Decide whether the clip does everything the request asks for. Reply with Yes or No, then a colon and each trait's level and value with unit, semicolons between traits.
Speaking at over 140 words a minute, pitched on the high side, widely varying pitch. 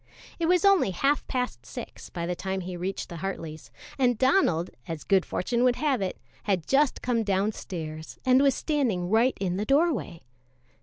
Yes: average, 175 wpm; high, 205 Hz; wide, 6.8 semitones